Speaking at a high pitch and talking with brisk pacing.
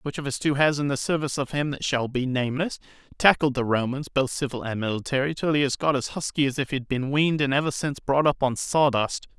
No: medium, 140 Hz; fast, 250 wpm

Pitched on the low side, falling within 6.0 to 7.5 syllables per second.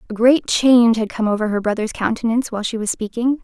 No: high, 230 Hz; 6.5 syllables/s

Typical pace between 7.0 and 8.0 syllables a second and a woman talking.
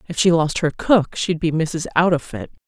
No: 4.9 syllables/s; female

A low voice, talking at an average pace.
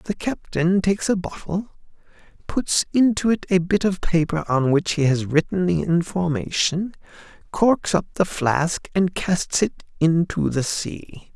No: medium, 170 Hz; average, 155 wpm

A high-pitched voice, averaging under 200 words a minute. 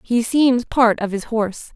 No: high, 230 Hz; fast, 205 wpm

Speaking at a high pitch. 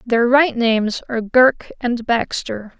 Yes: high, 240 Hz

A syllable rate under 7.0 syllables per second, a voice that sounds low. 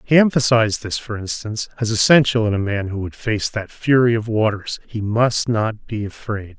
Yes: 5.1 syllables/s; low, 110 Hz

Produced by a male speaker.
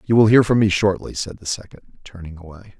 Yes: male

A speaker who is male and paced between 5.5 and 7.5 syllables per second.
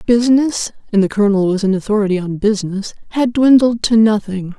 No: female; 6.0 syllables/s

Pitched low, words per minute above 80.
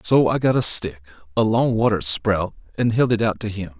Yes: low, 105 Hz; fast, 205 wpm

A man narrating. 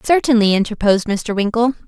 No: female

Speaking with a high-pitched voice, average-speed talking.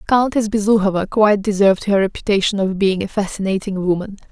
Yes: high, 200 Hz; average, 155 wpm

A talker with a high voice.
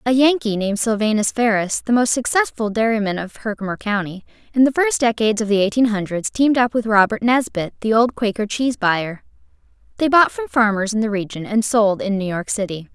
Yes: high, 220 Hz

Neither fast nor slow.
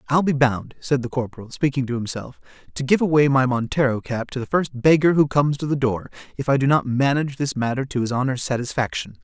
No: fast, 225 wpm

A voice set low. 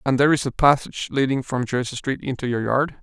Yes: low, 130 Hz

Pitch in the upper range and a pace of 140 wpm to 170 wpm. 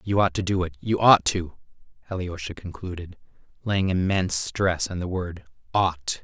No: very low, 90 Hz; average, 165 wpm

